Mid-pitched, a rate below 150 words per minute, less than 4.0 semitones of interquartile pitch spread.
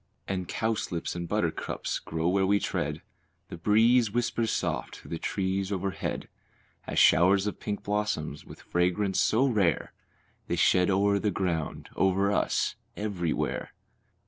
No: very low, 95 Hz; average, 140 wpm; average, 3.0 semitones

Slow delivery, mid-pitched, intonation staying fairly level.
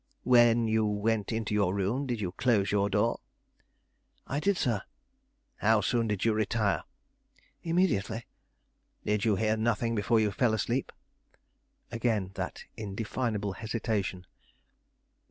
No: slow, 125 wpm; low, 110 Hz; narrow, 2.3 semitones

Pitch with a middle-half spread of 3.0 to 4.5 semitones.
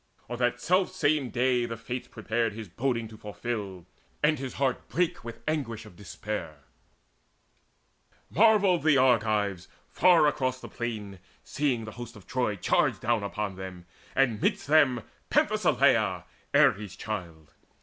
Yes: average, 4.2 semitones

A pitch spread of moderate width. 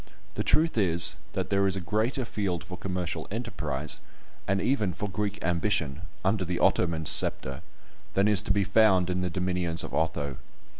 Yes: average, 3.2 semitones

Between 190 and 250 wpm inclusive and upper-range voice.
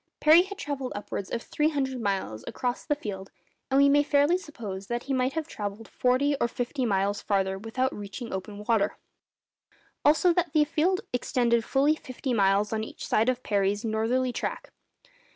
No: average, 175 wpm; high, 245 Hz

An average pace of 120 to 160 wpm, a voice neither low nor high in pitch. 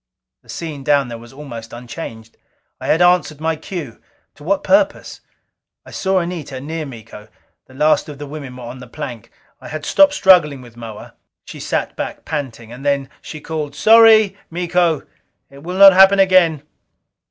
No: average, 175 wpm; medium, 150 Hz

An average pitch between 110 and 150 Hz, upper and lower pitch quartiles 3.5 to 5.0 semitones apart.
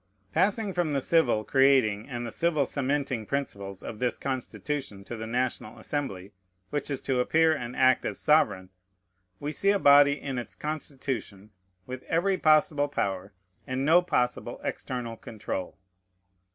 Yes: low, 135 Hz; average, 4.5 semitones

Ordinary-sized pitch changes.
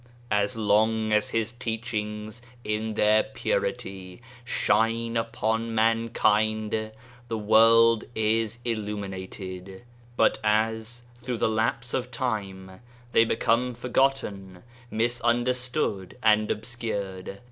No: narrow, 1.7 semitones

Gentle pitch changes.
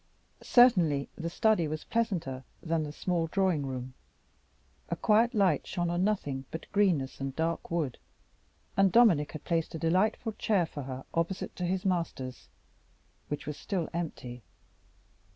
No: average, 4.7 semitones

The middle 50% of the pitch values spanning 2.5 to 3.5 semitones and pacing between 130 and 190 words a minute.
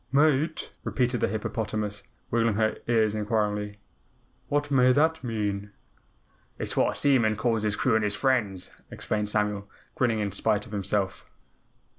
Yes: average, 3.2 semitones; average, 150 wpm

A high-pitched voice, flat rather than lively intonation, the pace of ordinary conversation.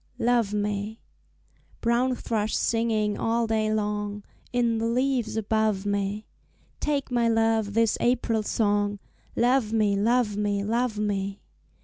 No: high, 220 Hz; narrow, 2.2 semitones; slow, 125 wpm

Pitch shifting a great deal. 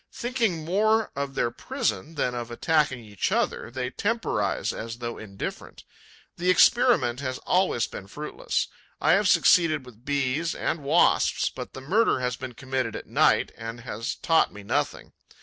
Yes: wide, 6.1 semitones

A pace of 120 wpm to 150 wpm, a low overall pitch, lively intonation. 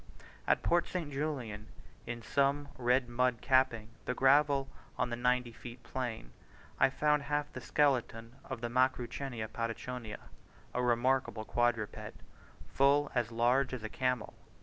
No: average, 140 wpm; low, 125 Hz; narrow, 2.6 semitones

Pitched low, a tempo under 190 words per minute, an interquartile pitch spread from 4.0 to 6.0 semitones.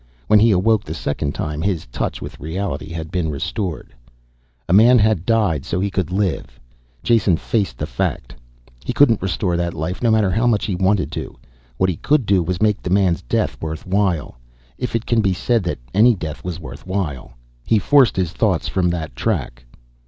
No: very low, 95 Hz; average, 195 wpm; average, 4.8 semitones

